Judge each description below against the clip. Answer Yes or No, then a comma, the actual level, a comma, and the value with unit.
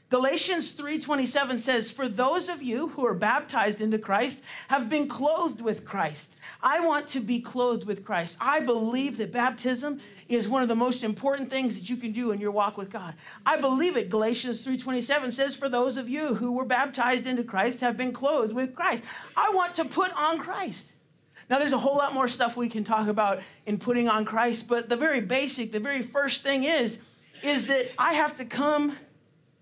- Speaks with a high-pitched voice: Yes, very high, 255 Hz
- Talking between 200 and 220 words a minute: Yes, fast, 205 wpm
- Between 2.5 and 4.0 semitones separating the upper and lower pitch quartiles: Yes, average, 3.6 semitones